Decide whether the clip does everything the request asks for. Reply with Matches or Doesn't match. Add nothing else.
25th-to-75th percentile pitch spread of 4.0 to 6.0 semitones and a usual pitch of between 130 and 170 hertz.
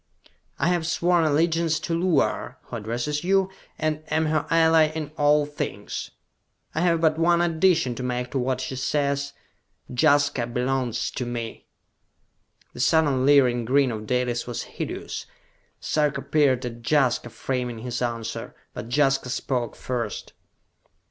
Matches